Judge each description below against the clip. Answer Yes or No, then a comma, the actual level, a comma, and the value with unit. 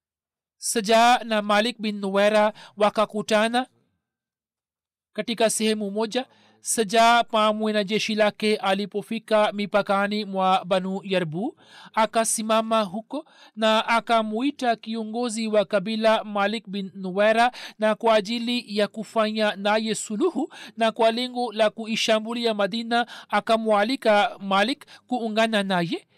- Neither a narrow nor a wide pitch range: No, narrow, 1.8 semitones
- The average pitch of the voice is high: Yes, high, 220 Hz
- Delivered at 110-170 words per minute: No, slow, 100 wpm